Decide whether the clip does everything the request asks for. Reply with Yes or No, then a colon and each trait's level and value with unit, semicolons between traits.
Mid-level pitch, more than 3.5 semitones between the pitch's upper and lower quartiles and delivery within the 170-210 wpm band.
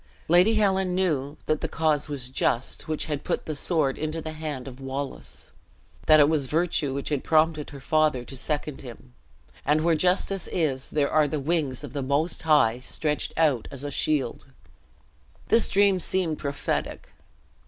No: medium, 150 Hz; average, 2.8 semitones; average, 175 wpm